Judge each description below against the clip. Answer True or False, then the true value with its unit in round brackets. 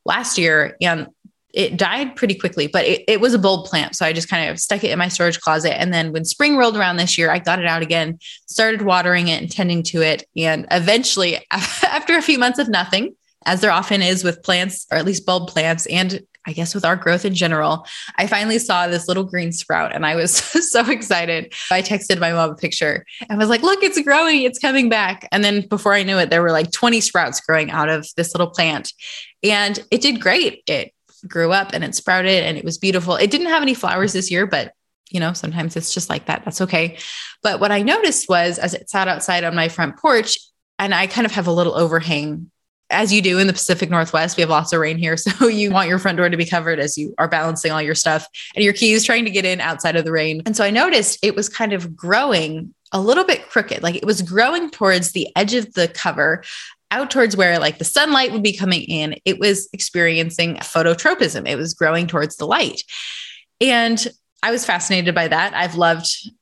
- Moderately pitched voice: True (180 Hz)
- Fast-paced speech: True (235 wpm)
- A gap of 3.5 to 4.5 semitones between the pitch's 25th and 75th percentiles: True (4.0 semitones)